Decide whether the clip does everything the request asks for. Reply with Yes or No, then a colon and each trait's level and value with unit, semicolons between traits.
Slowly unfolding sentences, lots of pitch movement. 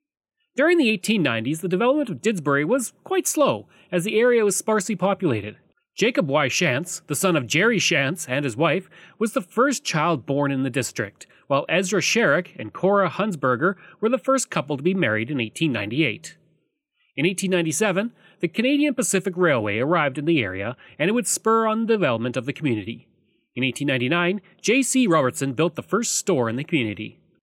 No: average, 175 wpm; wide, 7.6 semitones